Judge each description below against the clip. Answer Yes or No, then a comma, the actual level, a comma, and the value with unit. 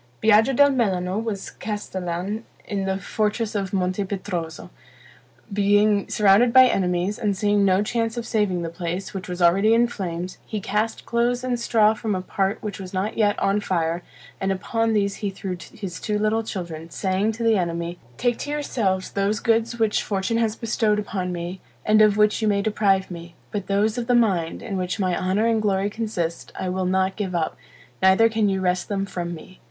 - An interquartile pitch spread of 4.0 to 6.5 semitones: No, average, 2.9 semitones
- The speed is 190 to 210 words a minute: Yes, average, 195 wpm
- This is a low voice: No, high, 200 Hz